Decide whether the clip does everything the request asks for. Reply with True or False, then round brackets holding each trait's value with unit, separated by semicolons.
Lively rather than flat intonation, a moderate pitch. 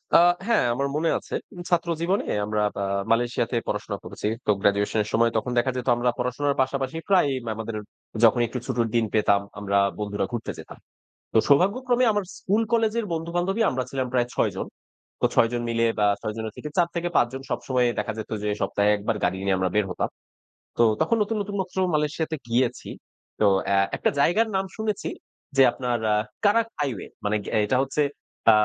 False (7.8 semitones; 125 Hz)